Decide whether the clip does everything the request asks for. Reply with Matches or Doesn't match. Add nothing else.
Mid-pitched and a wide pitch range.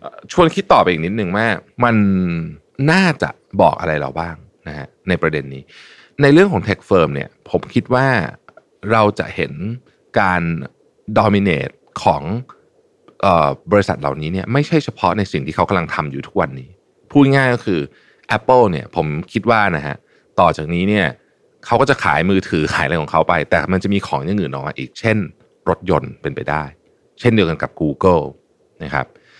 Doesn't match